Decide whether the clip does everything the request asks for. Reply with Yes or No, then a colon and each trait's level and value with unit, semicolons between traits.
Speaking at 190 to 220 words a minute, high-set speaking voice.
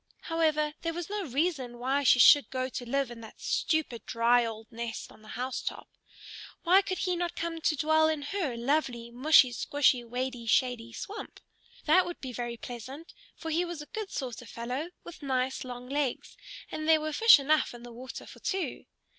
Yes: average, 195 wpm; very high, 275 Hz